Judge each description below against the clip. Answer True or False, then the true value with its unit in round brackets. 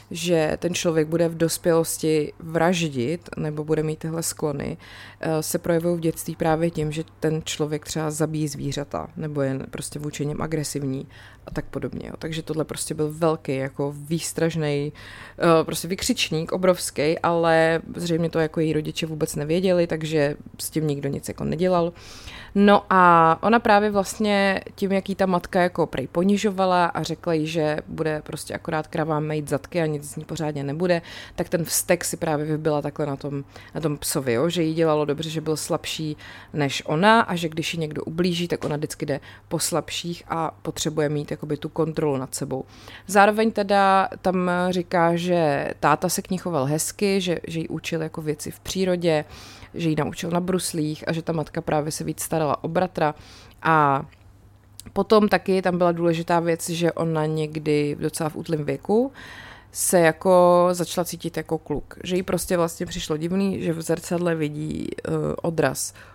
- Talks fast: True (180 wpm)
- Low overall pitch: False (160 Hz)